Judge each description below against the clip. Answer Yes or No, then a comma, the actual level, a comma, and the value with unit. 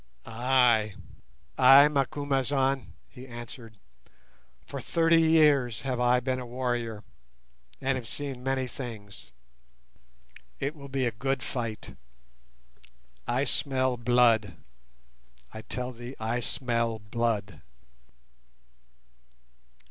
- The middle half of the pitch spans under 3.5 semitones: Yes, average, 3.1 semitones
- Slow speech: Yes, slow, 95 wpm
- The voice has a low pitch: Yes, low, 125 Hz